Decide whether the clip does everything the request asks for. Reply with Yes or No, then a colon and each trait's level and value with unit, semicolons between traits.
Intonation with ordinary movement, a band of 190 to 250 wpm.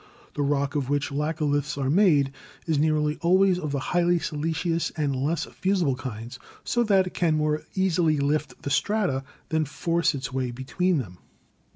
No: average, 3.5 semitones; average, 170 wpm